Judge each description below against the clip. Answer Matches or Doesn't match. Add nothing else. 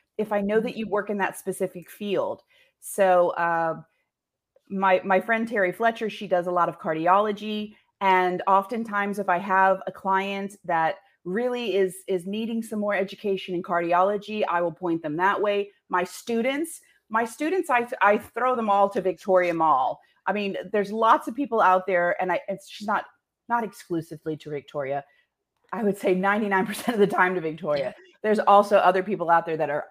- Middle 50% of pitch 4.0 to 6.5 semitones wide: Doesn't match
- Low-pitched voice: Doesn't match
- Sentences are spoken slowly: Doesn't match